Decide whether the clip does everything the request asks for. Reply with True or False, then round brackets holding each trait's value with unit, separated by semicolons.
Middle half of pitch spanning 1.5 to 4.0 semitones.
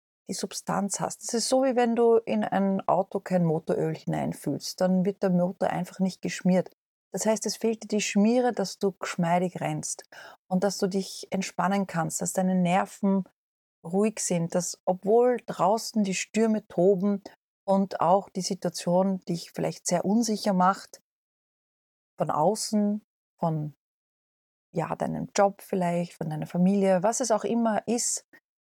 True (2.7 semitones)